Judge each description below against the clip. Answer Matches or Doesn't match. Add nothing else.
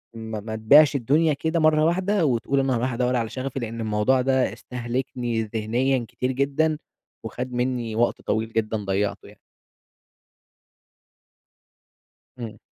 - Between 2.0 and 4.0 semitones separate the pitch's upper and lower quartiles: Matches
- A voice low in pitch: Matches